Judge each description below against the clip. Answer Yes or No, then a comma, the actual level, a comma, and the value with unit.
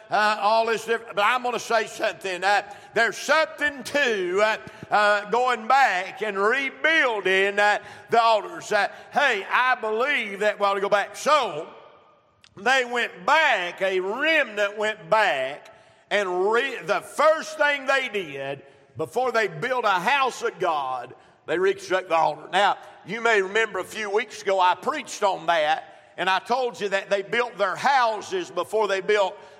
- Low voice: No, high, 215 Hz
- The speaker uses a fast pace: No, average, 170 wpm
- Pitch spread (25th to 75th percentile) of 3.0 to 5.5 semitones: Yes, average, 4.2 semitones